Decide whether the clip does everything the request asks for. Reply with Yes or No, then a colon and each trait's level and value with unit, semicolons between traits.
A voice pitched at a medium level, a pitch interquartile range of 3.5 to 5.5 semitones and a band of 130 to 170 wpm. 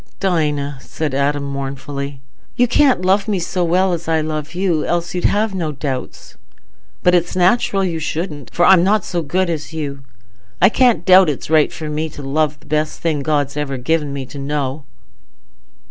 No: medium, 155 Hz; average, 4.0 semitones; average, 185 wpm